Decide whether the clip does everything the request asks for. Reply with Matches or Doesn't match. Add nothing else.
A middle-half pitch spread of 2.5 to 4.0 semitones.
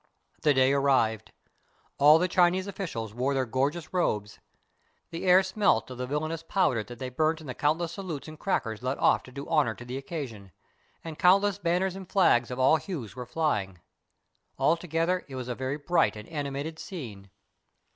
Doesn't match